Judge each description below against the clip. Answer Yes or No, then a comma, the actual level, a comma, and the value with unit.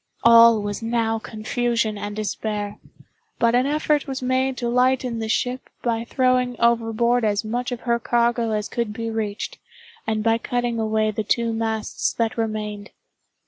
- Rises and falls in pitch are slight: Yes, narrow, 2.0 semitones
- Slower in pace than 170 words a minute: Yes, average, 155 wpm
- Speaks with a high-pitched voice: Yes, high, 230 Hz